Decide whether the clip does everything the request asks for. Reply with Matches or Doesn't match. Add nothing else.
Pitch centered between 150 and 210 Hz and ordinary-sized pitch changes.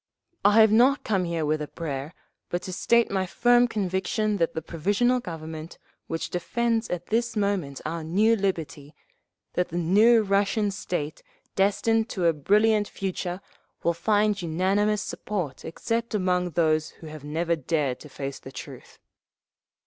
Matches